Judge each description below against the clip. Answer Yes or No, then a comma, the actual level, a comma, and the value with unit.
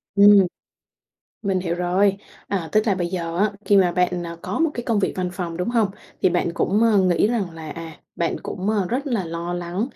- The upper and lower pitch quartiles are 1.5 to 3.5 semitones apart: Yes, average, 3.1 semitones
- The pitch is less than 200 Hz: Yes, medium, 185 Hz